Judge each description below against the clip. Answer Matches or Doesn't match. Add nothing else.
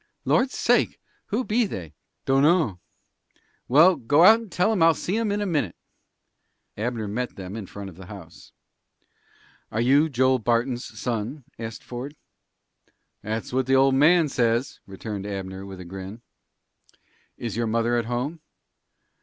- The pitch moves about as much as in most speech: Doesn't match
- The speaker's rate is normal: Matches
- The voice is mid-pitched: Doesn't match